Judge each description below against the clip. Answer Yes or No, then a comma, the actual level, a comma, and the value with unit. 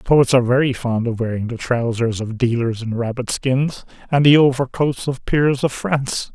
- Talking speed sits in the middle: Yes, average, 190 wpm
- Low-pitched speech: Yes, low, 125 Hz